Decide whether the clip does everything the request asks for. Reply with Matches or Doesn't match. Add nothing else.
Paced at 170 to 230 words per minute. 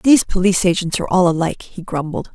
Matches